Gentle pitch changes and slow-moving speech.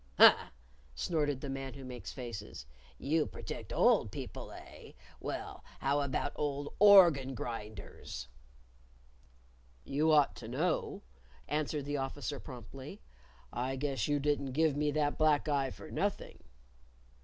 Yes: narrow, 2.3 semitones; slow, 130 wpm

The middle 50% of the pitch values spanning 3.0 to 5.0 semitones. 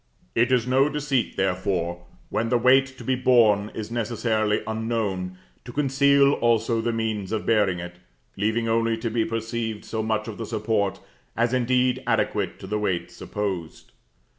No: narrow, 2.6 semitones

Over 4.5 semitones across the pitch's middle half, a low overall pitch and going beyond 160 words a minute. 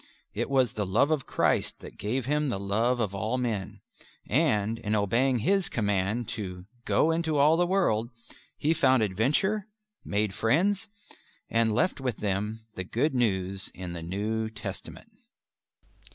No: average, 5.3 semitones; low, 115 Hz; average, 150 wpm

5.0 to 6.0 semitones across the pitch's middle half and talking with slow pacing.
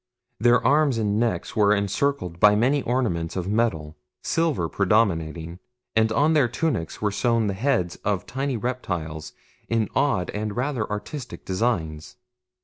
No: wide, 5.6 semitones; average, 145 wpm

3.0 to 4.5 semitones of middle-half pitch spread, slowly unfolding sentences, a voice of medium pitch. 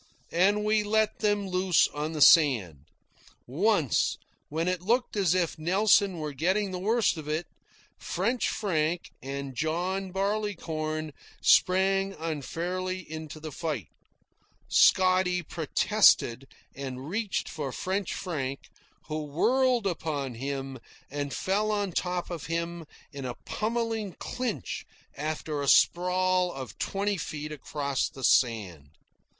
No: average, 4.9 semitones; slow, 125 wpm; medium, 170 Hz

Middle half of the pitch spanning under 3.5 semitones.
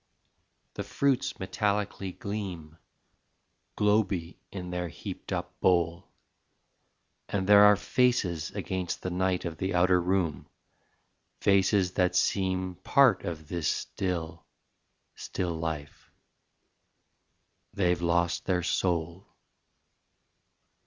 Yes: narrow, 2.4 semitones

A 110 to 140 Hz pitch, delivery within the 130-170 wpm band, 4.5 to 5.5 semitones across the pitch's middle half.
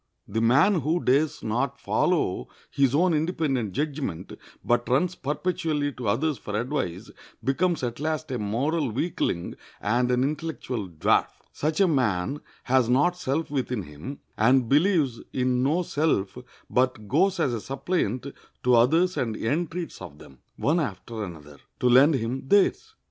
Yes: low, 135 Hz; average, 150 wpm; average, 5.2 semitones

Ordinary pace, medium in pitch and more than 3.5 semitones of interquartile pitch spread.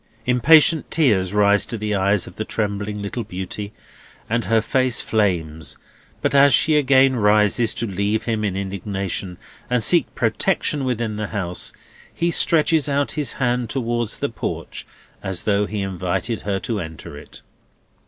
No: average, 155 wpm; low, 110 Hz; average, 4.0 semitones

